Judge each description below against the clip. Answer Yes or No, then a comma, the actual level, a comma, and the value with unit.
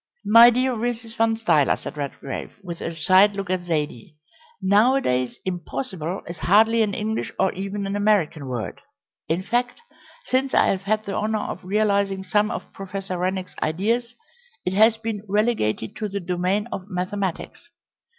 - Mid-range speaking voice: No, high, 195 Hz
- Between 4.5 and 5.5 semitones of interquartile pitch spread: No, average, 3.5 semitones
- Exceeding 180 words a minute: No, average, 160 wpm